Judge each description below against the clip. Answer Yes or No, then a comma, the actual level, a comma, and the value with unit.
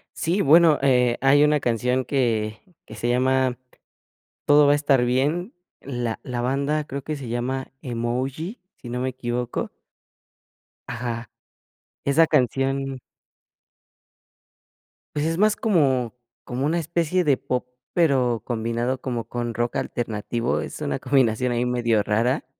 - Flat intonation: No, average, 3.1 semitones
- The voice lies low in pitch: Yes, low, 130 Hz